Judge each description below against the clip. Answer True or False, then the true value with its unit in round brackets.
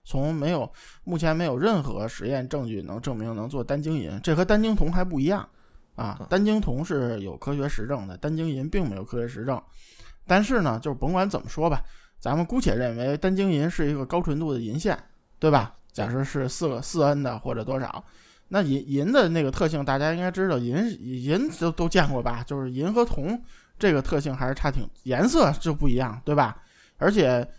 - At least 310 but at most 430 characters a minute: False (300 characters per minute)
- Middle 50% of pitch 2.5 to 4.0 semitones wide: False (4.8 semitones)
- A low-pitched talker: False (145 Hz)